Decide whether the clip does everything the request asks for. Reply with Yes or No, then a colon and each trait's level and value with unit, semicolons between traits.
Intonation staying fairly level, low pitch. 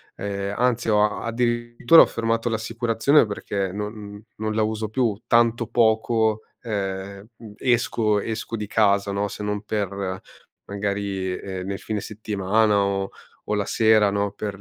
Yes: narrow, 2.2 semitones; low, 105 Hz